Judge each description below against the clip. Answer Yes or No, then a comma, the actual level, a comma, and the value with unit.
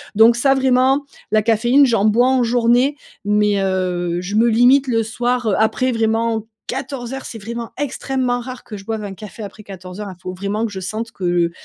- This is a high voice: Yes, high, 225 Hz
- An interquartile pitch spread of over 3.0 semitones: Yes, average, 3.5 semitones